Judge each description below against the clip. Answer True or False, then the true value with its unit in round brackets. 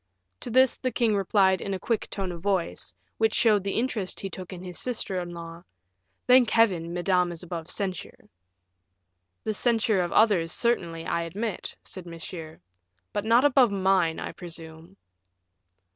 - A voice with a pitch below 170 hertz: False (190 Hz)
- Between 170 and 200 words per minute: False (160 wpm)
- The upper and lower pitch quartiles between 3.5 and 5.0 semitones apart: True (4.2 semitones)